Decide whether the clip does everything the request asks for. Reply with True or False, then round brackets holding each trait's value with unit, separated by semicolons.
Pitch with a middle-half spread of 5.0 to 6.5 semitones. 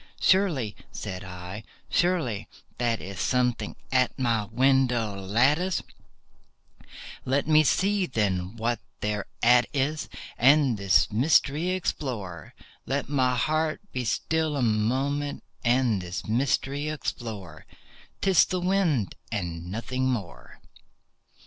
True (5.6 semitones)